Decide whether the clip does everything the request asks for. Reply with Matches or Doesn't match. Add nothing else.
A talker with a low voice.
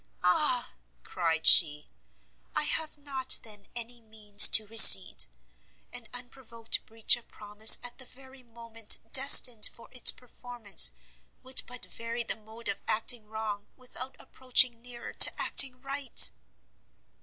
Doesn't match